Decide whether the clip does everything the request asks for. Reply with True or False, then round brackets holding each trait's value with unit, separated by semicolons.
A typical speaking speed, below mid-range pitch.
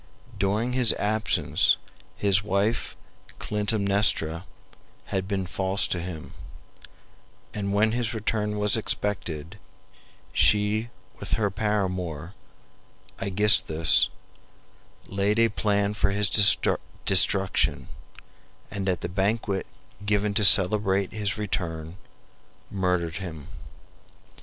False (95 wpm; 100 Hz)